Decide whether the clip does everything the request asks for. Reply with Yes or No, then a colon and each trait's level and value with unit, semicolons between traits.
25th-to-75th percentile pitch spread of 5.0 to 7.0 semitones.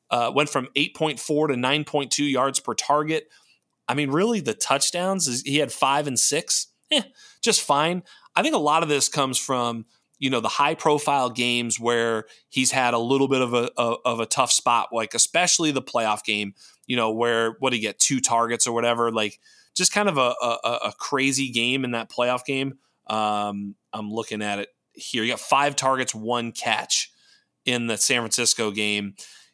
No: average, 3.8 semitones